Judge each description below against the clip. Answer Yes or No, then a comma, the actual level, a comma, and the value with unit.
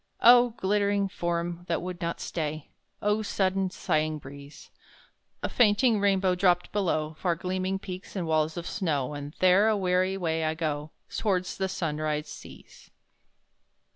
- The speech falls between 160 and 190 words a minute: No, average, 145 wpm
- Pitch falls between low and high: Yes, medium, 180 Hz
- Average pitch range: Yes, average, 3.7 semitones